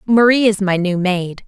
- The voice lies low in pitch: No, high, 200 Hz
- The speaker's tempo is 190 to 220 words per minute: Yes, fast, 205 wpm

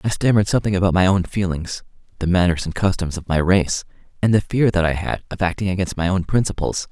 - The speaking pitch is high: No, very low, 95 Hz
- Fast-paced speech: Yes, fast, 210 wpm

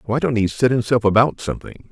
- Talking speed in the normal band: No, fast, 220 wpm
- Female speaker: No, male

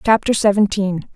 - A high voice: Yes, high, 200 Hz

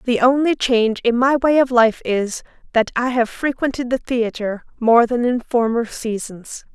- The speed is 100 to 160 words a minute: No, average, 180 wpm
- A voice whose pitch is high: Yes, high, 240 Hz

